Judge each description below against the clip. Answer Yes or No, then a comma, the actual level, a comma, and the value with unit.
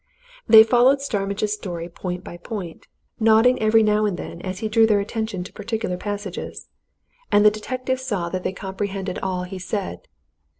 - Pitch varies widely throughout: No, average, 3.0 semitones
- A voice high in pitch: Yes, high, 205 Hz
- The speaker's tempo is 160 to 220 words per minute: Yes, average, 170 wpm